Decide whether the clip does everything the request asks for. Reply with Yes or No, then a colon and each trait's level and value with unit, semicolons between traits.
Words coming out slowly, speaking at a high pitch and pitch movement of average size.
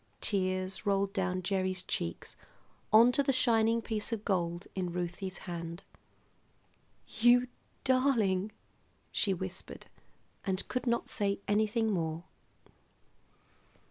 Yes: slow, 105 wpm; high, 195 Hz; average, 3.5 semitones